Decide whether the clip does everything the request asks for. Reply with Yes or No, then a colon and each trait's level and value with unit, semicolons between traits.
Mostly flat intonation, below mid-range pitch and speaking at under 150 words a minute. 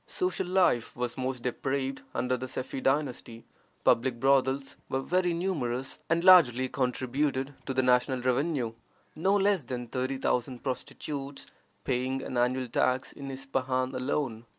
Yes: narrow, 1.9 semitones; low, 130 Hz; average, 140 wpm